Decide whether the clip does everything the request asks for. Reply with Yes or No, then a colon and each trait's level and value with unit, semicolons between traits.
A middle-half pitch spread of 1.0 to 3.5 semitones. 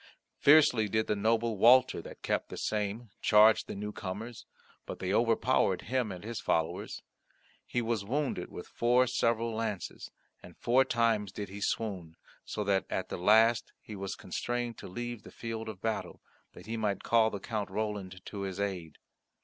Yes: average, 2.9 semitones